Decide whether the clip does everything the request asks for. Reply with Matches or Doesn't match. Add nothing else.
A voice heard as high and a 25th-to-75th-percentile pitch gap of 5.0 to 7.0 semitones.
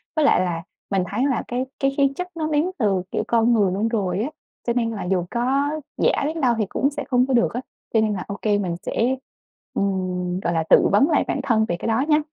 Matches